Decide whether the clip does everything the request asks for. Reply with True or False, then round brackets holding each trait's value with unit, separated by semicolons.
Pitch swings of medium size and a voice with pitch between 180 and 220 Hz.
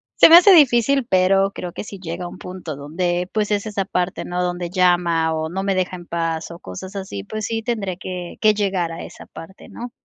True (3.0 semitones; 185 Hz)